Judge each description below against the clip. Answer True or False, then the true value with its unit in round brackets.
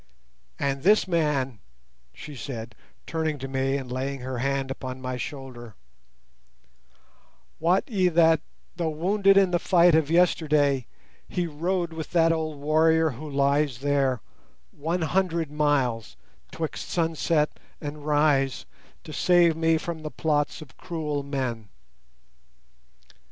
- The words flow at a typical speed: False (130 wpm)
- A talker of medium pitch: True (150 Hz)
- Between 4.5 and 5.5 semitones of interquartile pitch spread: False (3.4 semitones)